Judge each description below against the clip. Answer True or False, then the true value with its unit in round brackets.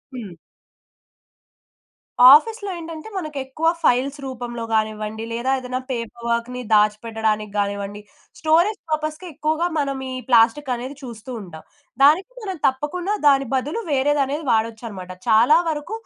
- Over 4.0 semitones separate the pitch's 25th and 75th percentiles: True (5.5 semitones)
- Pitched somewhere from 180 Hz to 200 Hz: False (260 Hz)